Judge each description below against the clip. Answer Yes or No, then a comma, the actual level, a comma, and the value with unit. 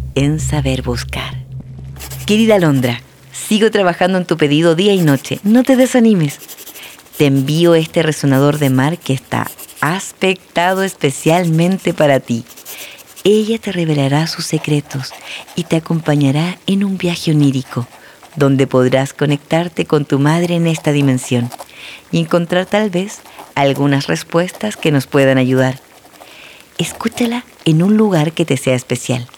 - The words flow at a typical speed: Yes, average, 135 wpm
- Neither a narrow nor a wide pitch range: Yes, average, 4.7 semitones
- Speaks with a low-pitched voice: No, medium, 155 Hz